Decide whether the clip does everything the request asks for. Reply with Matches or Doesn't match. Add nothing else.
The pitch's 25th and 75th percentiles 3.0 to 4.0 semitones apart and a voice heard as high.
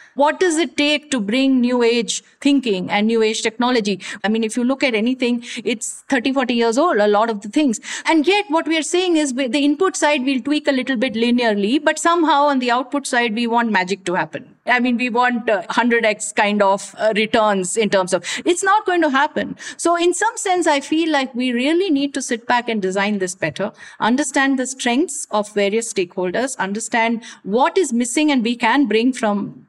Doesn't match